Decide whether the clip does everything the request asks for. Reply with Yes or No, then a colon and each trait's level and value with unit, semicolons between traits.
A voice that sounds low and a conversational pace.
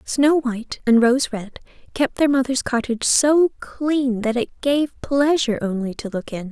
No: very high, 255 Hz; average, 175 wpm